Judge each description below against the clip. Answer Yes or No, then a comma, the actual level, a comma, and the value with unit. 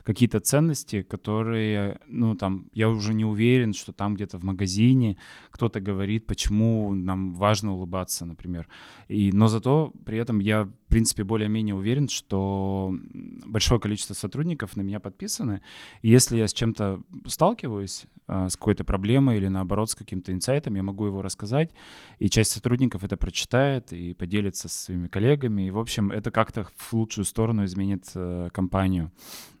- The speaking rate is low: No, average, 155 wpm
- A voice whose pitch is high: No, low, 105 Hz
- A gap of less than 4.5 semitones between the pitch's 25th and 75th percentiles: Yes, average, 2.7 semitones